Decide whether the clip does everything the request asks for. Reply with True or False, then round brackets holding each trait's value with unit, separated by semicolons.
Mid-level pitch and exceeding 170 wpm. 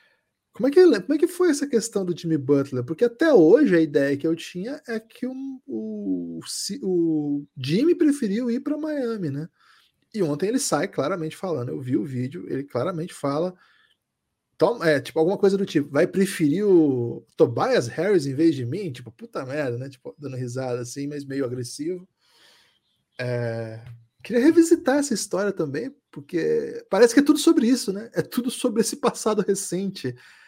True (175 Hz; 180 wpm)